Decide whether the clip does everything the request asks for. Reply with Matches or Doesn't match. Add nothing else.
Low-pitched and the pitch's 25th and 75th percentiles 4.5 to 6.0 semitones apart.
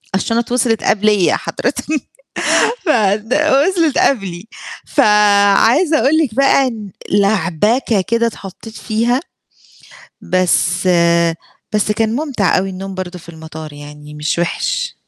Doesn't match